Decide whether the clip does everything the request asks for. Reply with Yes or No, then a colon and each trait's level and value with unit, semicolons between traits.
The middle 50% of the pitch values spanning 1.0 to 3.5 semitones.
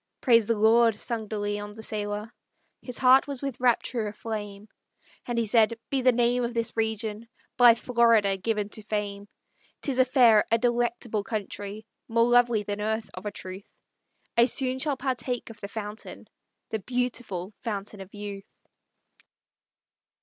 Yes: narrow, 2.6 semitones